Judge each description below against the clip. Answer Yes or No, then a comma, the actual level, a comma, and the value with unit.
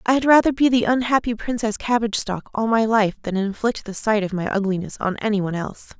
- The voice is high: Yes, high, 220 Hz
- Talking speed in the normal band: No, fast, 220 wpm